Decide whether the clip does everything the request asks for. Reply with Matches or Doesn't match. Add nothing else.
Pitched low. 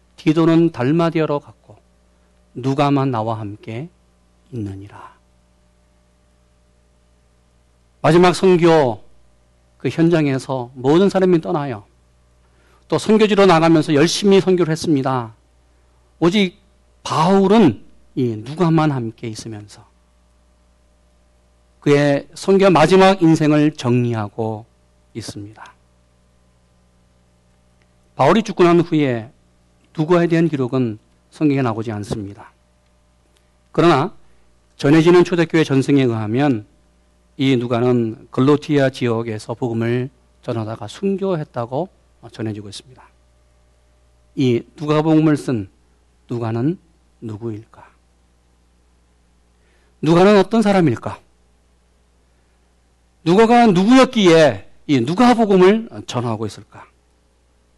Matches